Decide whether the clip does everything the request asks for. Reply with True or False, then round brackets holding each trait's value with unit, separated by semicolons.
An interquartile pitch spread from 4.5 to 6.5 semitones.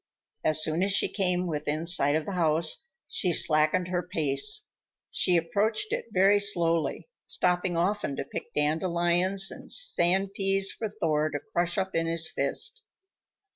False (3.5 semitones)